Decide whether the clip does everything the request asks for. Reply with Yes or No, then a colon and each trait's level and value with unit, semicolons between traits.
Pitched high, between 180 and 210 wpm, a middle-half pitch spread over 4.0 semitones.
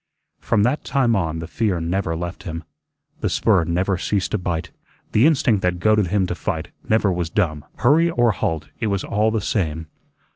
No: very low, 95 Hz; average, 190 wpm; average, 4.5 semitones